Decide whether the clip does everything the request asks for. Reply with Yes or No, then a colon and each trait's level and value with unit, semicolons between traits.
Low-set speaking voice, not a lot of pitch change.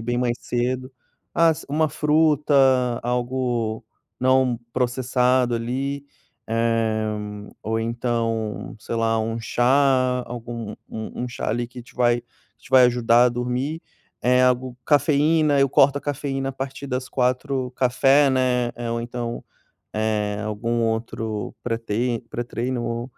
Yes: low, 125 Hz; narrow, 2.1 semitones